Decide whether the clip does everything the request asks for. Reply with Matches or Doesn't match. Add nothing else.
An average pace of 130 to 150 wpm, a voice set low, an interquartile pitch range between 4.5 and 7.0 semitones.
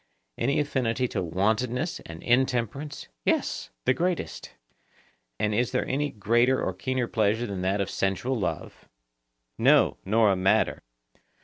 Matches